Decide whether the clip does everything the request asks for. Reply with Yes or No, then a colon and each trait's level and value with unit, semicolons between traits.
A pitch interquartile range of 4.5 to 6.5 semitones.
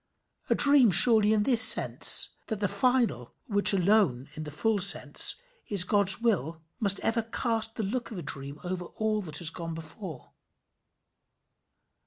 Yes: average, 5.1 semitones